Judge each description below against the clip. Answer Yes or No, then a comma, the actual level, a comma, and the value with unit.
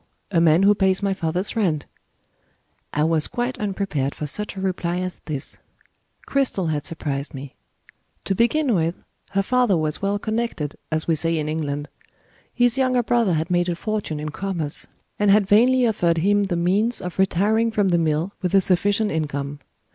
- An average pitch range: Yes, average, 4.7 semitones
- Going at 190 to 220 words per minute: No, average, 180 wpm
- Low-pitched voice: No, medium, 185 Hz